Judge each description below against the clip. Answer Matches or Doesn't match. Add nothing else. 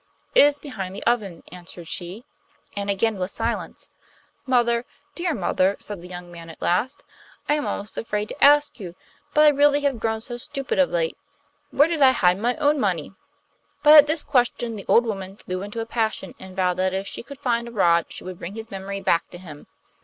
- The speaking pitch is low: Doesn't match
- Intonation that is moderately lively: Doesn't match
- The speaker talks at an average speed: Doesn't match